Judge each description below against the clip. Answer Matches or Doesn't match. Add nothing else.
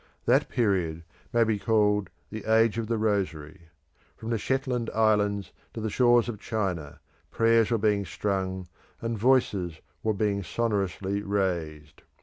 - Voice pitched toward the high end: Doesn't match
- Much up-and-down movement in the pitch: Doesn't match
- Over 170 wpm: Doesn't match